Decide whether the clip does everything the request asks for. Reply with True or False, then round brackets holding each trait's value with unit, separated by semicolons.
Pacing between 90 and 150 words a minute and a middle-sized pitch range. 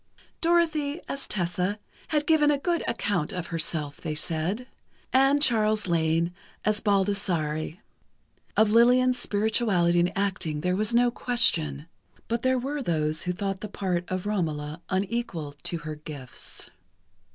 False (140 wpm; 6.4 semitones)